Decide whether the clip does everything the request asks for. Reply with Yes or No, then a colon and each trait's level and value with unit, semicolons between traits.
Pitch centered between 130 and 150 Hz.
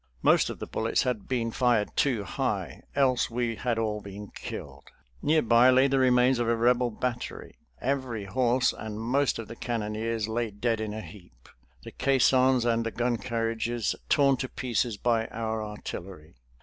No: low, 115 Hz